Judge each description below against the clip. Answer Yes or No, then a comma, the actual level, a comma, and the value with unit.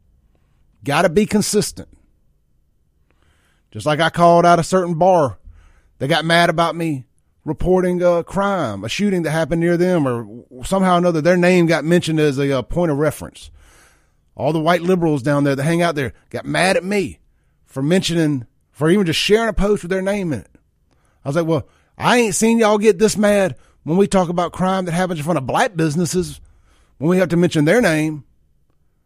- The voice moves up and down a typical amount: No, wide, 6.5 semitones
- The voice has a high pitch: No, medium, 165 Hz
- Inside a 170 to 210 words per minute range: Yes, average, 195 wpm